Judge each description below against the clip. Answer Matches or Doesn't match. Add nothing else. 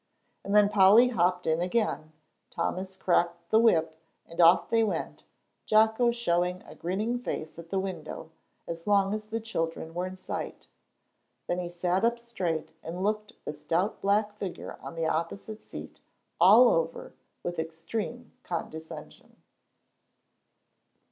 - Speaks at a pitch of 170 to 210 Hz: Matches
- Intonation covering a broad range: Doesn't match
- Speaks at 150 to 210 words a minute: Doesn't match